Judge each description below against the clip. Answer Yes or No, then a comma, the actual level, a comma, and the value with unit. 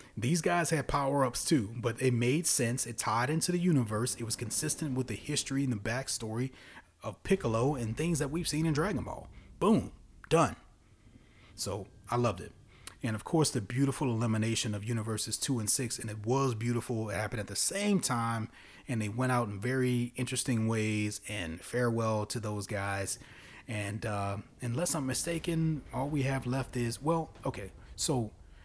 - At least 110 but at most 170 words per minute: No, average, 180 wpm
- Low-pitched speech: Yes, low, 120 Hz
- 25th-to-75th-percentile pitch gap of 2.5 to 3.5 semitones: No, average, 4.0 semitones